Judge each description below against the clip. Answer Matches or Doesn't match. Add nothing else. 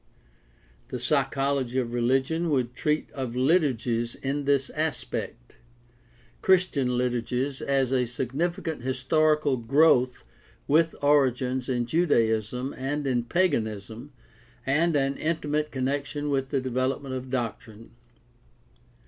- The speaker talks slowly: Matches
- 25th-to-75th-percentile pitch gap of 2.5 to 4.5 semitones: Matches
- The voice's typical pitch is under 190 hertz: Matches